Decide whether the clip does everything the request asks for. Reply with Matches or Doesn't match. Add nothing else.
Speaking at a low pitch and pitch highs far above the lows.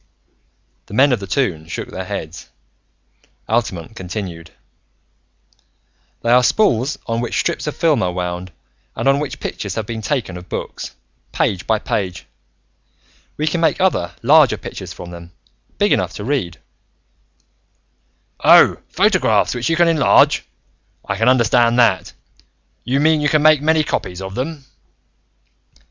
Matches